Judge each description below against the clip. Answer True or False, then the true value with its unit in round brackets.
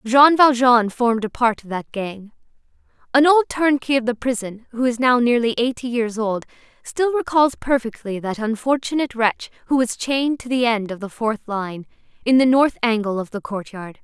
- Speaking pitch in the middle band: False (240 Hz)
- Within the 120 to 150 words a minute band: False (190 wpm)